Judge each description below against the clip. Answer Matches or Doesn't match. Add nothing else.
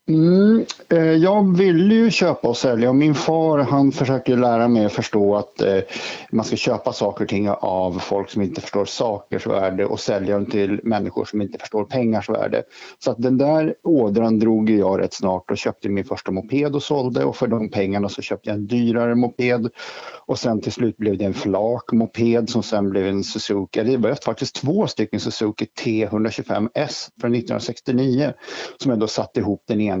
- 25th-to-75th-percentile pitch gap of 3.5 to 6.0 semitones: Matches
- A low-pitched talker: Matches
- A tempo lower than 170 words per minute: Doesn't match